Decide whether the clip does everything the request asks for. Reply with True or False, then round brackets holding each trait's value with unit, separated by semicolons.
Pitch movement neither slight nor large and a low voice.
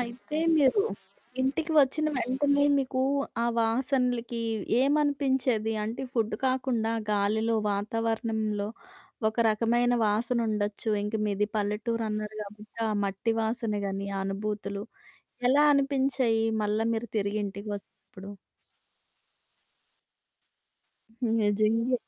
False (3.5 semitones; 225 Hz)